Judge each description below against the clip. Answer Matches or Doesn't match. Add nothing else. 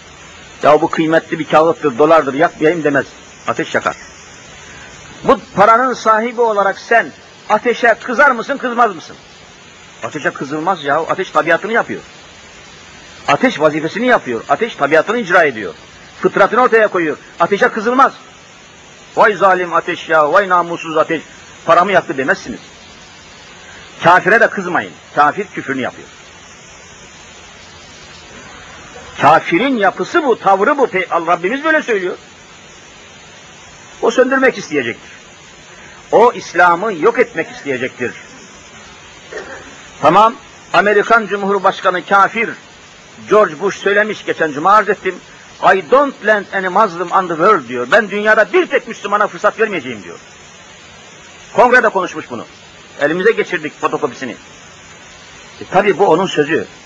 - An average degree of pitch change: Doesn't match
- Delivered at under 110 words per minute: Doesn't match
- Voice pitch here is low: Doesn't match